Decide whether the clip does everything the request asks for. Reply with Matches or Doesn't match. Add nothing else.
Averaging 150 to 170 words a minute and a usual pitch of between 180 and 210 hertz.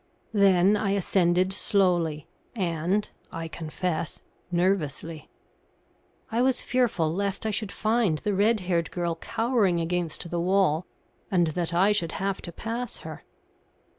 Doesn't match